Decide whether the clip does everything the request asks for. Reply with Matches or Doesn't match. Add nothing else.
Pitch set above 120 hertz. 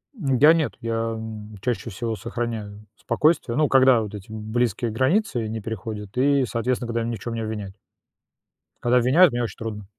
Doesn't match